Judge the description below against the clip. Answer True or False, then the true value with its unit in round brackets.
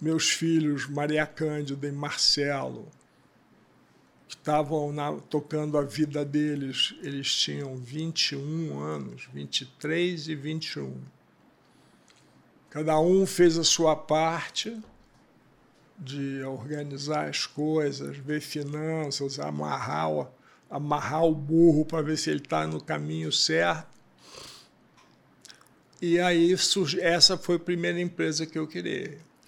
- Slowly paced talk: True (110 wpm)